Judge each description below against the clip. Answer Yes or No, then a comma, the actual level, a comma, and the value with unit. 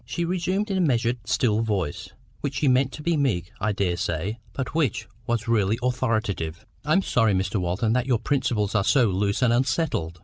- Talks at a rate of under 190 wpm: No, average, 195 wpm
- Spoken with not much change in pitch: No, average, 5.2 semitones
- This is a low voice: Yes, low, 115 Hz